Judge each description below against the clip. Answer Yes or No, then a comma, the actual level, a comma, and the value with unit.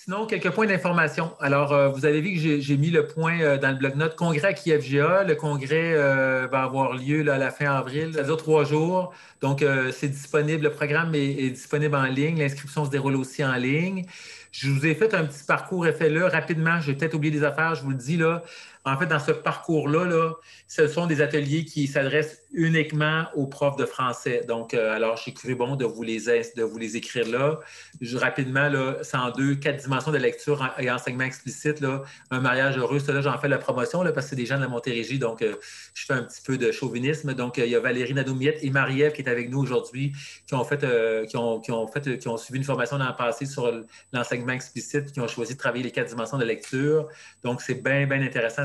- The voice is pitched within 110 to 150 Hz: Yes, medium, 140 Hz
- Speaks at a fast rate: Yes, fast, 240 wpm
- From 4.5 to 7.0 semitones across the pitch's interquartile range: No, average, 3.0 semitones